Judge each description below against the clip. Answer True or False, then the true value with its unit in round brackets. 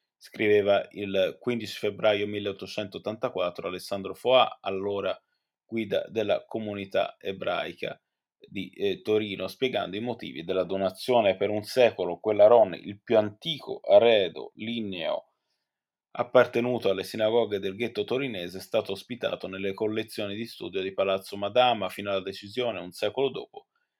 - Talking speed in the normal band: True (130 wpm)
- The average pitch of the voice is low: True (105 Hz)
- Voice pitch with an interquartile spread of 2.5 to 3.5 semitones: True (2.9 semitones)